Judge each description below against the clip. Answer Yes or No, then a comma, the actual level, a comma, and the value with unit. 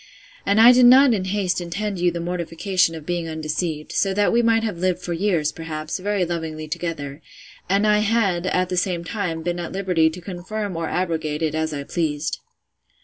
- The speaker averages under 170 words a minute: No, average, 200 wpm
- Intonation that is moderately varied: Yes, average, 3.5 semitones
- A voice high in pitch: No, medium, 175 Hz